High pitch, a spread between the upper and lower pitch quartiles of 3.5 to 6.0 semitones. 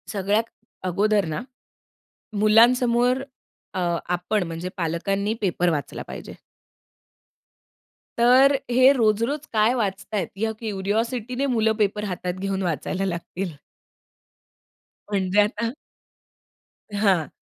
Yes: high, 210 Hz; average, 3.8 semitones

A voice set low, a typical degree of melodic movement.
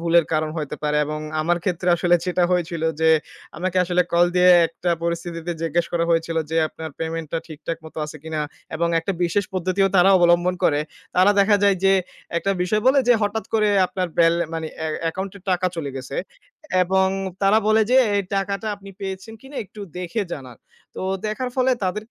No: medium, 180 Hz; average, 3.0 semitones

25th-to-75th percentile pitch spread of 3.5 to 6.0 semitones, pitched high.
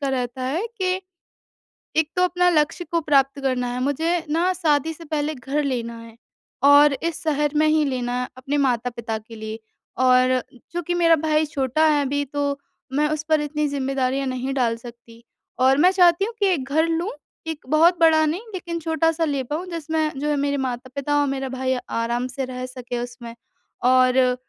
Yes: average, 3.9 semitones; very high, 285 Hz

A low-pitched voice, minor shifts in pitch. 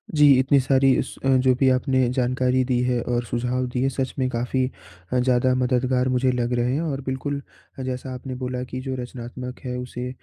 Yes: low, 130 Hz; narrow, 0.9 semitones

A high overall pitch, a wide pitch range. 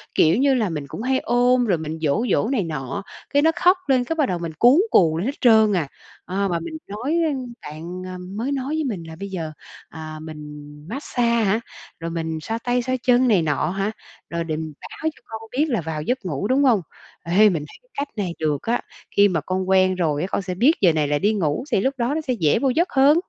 Yes: high, 200 Hz; wide, 7.3 semitones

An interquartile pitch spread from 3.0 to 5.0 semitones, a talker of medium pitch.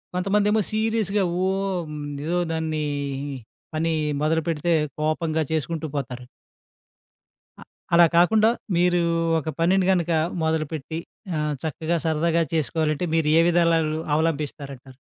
No: narrow, 2.4 semitones; medium, 165 Hz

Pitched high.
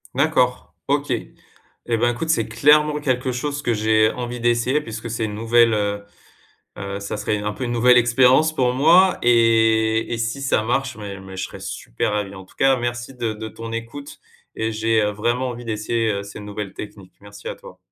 No: low, 115 Hz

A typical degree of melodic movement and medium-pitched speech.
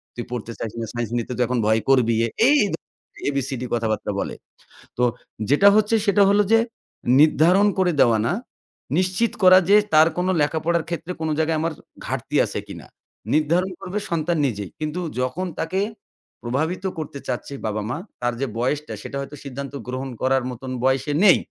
No: wide, 6.2 semitones; medium, 145 Hz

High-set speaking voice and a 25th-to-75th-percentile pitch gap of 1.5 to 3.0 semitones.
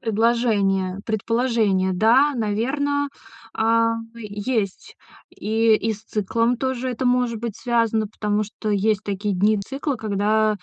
Yes: high, 220 Hz; narrow, 2.4 semitones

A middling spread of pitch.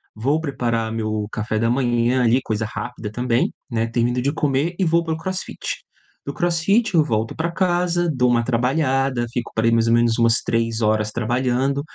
Yes: average, 4.7 semitones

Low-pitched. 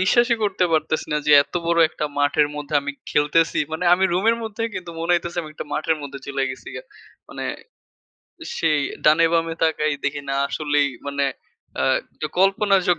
No: medium, 160 Hz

